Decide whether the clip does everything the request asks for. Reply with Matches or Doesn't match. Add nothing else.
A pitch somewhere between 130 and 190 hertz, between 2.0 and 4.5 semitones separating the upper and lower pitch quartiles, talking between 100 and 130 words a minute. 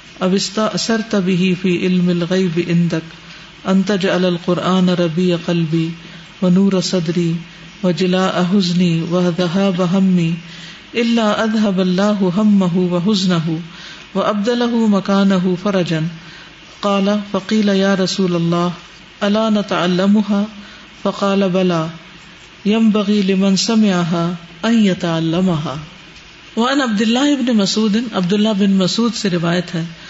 Matches